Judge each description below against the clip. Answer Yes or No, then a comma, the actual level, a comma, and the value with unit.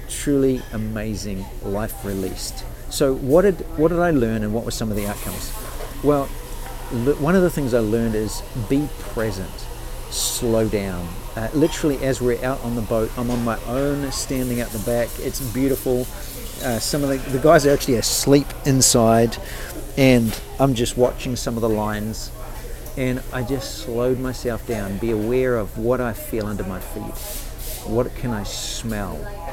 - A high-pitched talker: No, low, 120 Hz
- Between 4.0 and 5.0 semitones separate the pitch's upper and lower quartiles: No, average, 3.3 semitones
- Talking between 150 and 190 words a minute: Yes, average, 175 wpm